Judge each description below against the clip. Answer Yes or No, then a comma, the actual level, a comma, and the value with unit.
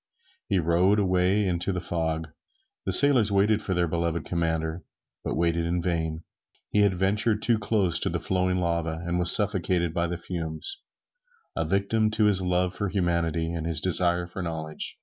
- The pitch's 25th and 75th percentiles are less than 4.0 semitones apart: Yes, average, 2.7 semitones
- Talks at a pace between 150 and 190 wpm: Yes, average, 175 wpm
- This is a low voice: Yes, very low, 90 Hz